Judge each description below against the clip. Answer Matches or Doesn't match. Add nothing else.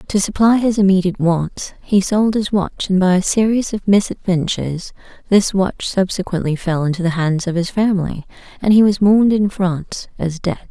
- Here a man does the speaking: Doesn't match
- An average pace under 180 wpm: Doesn't match